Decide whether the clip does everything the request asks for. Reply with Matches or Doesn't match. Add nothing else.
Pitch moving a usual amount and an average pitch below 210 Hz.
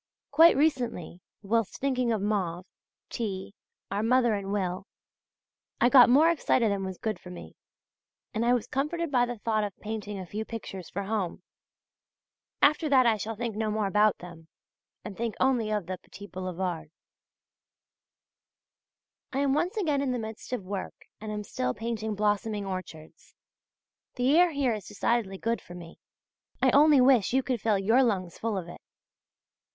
Doesn't match